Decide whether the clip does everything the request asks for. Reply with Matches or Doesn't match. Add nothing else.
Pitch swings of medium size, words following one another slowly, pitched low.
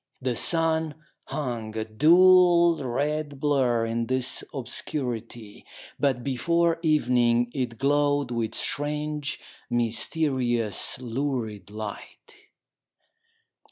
Matches